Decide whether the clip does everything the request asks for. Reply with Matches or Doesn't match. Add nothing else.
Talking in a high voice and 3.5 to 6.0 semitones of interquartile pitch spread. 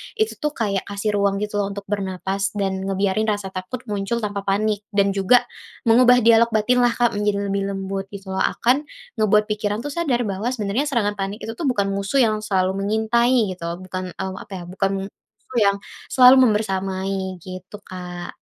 Doesn't match